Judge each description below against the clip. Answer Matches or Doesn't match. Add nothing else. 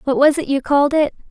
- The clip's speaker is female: Matches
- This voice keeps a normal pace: Doesn't match